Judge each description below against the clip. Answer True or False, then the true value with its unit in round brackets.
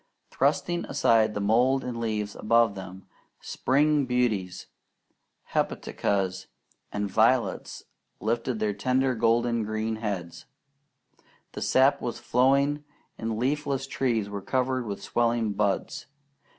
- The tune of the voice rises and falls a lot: False (3.8 semitones)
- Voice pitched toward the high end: False (115 Hz)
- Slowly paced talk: True (110 wpm)